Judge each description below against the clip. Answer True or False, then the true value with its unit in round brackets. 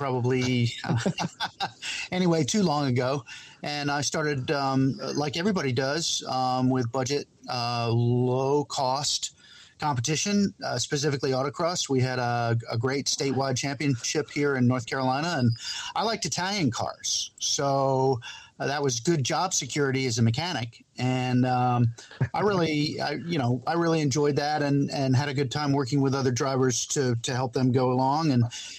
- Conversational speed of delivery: True (160 wpm)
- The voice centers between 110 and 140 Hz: True (135 Hz)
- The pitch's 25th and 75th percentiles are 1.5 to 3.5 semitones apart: True (2.6 semitones)